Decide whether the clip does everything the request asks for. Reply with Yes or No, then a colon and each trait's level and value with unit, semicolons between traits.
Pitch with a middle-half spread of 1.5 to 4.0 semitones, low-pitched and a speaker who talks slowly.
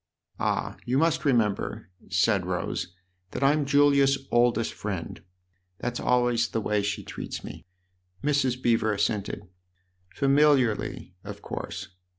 No: average, 4.9 semitones; low, 120 Hz; slow, 125 wpm